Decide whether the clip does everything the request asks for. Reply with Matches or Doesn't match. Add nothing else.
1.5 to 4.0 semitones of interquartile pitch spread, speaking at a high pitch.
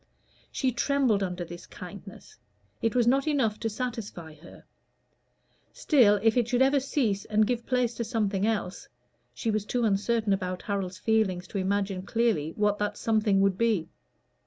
Matches